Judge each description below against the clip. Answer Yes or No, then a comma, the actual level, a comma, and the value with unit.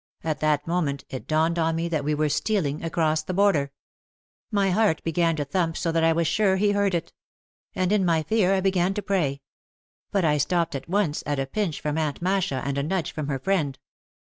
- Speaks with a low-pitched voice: No, medium, 165 Hz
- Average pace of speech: No, fast, 220 wpm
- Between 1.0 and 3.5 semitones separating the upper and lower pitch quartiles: No, average, 4.1 semitones